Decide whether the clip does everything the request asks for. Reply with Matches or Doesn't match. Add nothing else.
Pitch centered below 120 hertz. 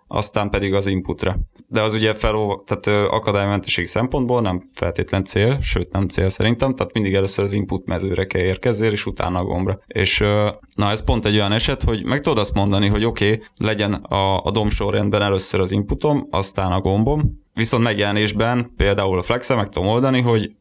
Matches